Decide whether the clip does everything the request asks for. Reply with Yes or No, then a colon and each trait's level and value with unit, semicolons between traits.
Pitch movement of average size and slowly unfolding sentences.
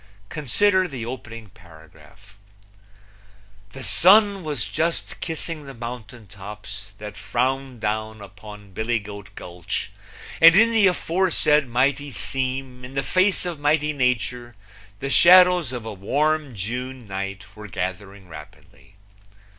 No: wide, 6.5 semitones; slow, 125 wpm